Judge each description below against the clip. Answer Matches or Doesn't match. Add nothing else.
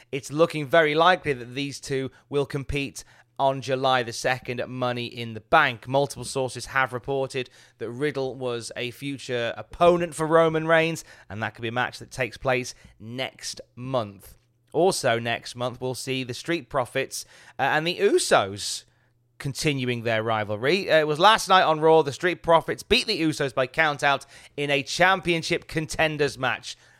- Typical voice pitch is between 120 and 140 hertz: Matches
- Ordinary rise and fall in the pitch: Matches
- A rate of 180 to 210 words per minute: Doesn't match